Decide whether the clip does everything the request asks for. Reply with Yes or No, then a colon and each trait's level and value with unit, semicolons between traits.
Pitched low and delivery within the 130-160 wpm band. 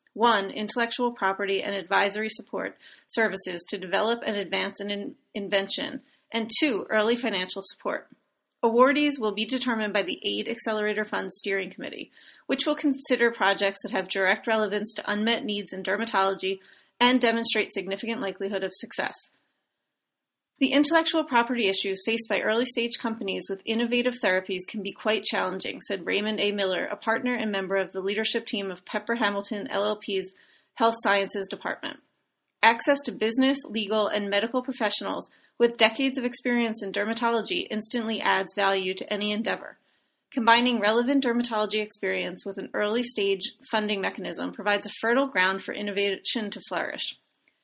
No: high, 215 Hz; average, 150 wpm